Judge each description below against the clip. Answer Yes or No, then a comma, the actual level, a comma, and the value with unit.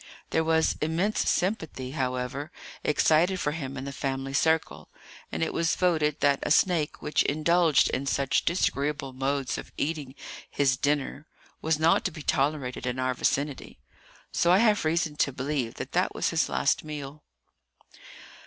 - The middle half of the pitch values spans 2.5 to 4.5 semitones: Yes, average, 2.9 semitones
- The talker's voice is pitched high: No, medium, 150 Hz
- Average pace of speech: Yes, average, 160 wpm